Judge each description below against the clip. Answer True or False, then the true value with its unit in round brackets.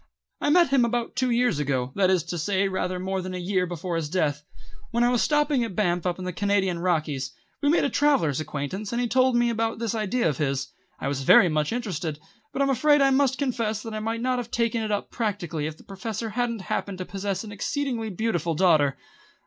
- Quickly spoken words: True (230 wpm)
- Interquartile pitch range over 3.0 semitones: True (5.6 semitones)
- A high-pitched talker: True (200 Hz)